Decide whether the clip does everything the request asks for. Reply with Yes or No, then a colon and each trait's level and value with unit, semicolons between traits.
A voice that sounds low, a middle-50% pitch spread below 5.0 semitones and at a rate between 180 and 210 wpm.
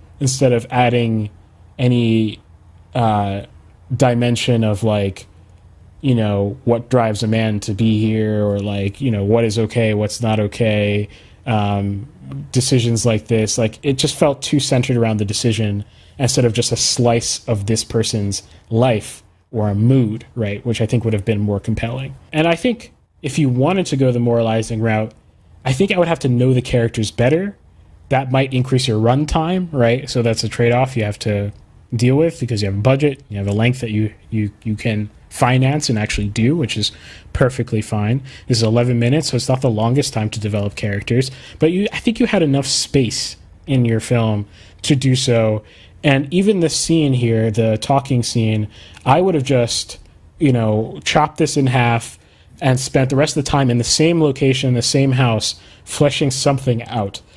Yes: low, 115 Hz; average, 3.8 semitones; average, 190 wpm